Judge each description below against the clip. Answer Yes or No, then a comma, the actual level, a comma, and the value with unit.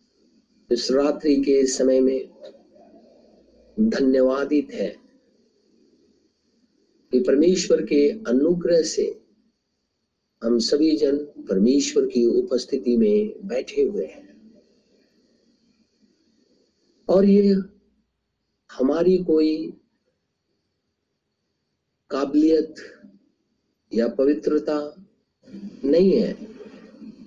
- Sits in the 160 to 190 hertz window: Yes, medium, 185 Hz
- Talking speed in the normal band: No, slow, 65 wpm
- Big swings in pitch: Yes, wide, 8.1 semitones